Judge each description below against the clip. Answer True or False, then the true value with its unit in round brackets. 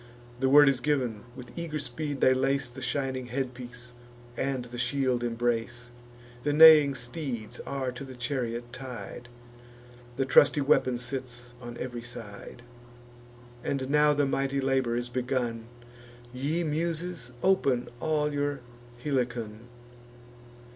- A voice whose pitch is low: True (130 Hz)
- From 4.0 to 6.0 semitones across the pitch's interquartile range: False (2.7 semitones)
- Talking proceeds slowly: True (125 wpm)